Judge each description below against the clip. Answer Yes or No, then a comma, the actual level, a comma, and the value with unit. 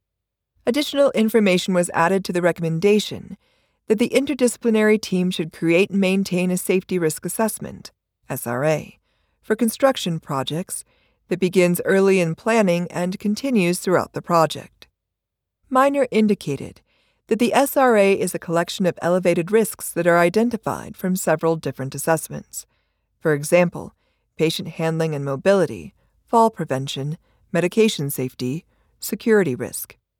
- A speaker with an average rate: No, slow, 125 wpm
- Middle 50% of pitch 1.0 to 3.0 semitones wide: No, average, 5.2 semitones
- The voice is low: No, medium, 180 Hz